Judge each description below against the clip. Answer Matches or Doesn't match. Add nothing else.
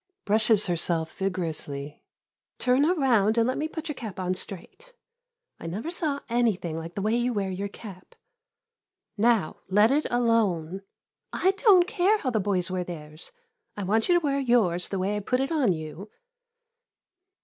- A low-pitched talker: Doesn't match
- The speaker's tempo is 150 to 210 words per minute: Matches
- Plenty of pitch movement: Matches